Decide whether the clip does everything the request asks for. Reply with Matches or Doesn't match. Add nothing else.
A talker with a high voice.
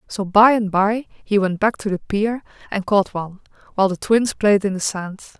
Matches